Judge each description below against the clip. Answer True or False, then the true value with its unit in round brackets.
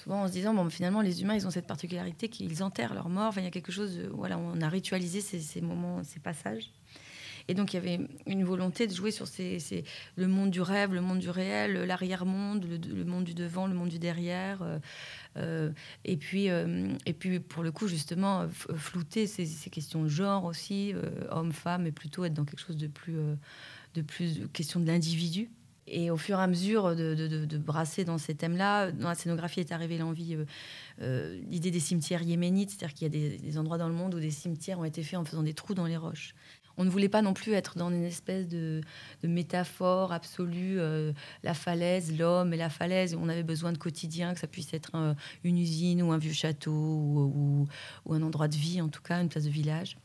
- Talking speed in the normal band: False (235 wpm)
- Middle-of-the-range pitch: True (170 Hz)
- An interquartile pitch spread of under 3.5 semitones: True (2.7 semitones)